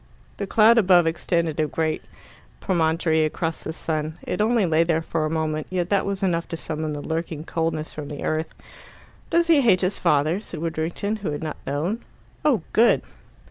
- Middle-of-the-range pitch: Yes, medium, 165 Hz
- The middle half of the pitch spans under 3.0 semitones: No, average, 3.5 semitones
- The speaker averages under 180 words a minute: No, average, 185 wpm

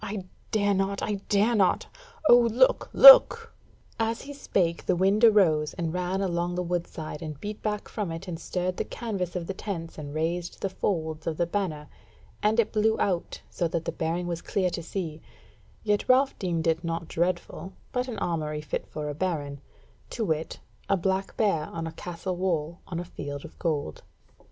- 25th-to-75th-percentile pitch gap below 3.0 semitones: No, average, 3.7 semitones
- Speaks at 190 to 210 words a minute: Yes, average, 195 wpm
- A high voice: No, medium, 180 Hz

